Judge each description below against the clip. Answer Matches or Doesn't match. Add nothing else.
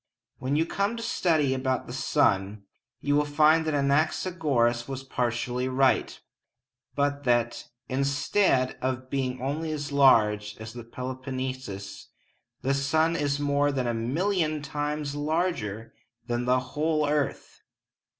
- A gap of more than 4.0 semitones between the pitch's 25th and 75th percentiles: Doesn't match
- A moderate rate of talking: Doesn't match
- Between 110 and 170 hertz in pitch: Matches